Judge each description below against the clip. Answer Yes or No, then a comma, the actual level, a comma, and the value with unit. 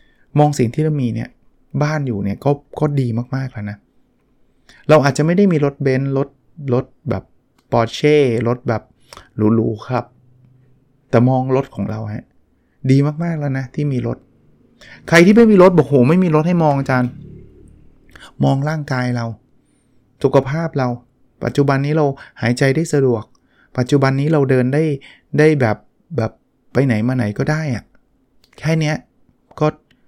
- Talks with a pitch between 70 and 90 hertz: No, low, 130 Hz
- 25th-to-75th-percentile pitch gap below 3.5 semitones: No, average, 3.8 semitones